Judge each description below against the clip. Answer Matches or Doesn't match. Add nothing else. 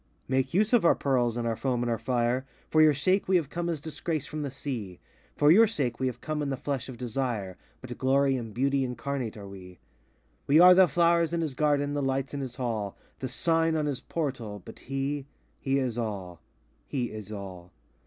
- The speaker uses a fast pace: Matches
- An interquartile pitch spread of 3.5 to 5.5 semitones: Matches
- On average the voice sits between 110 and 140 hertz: Matches